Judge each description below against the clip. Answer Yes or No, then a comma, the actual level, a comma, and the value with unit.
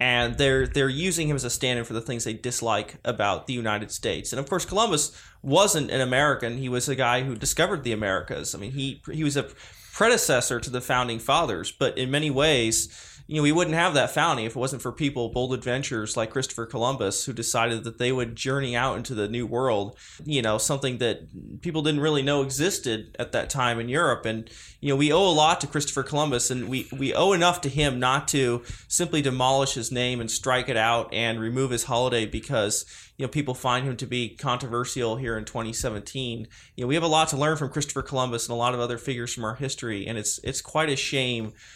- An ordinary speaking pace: No, fast, 230 wpm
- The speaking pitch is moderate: No, low, 125 Hz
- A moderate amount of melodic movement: Yes, average, 3.1 semitones